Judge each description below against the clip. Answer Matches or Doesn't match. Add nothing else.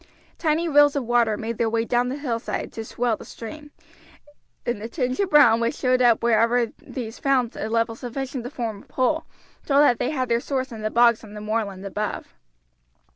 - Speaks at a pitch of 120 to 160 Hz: Doesn't match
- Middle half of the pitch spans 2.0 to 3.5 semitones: Matches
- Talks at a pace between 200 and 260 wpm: Matches